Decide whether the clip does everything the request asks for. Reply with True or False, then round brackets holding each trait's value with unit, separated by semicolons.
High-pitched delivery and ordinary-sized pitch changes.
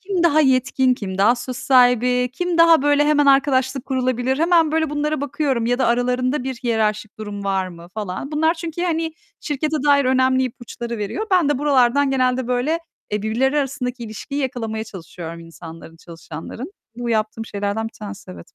True (255 Hz; 4.8 semitones)